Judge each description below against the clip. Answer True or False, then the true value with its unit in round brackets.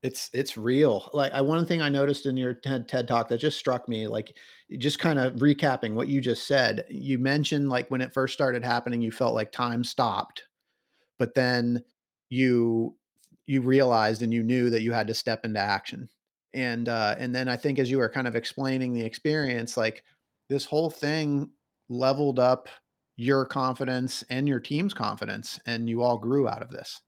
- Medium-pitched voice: False (130 Hz)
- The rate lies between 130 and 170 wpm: False (195 wpm)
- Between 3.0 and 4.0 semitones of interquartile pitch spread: False (2.6 semitones)